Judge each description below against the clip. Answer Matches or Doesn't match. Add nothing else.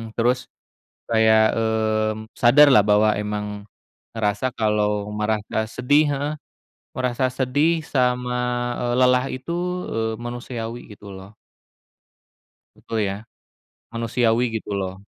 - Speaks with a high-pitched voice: Doesn't match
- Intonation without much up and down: Doesn't match